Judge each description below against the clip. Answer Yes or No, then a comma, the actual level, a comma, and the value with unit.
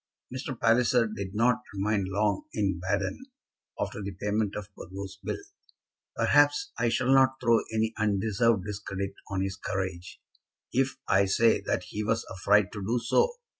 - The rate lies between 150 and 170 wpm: Yes, average, 155 wpm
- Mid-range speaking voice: No, low, 105 Hz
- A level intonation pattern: No, average, 3.1 semitones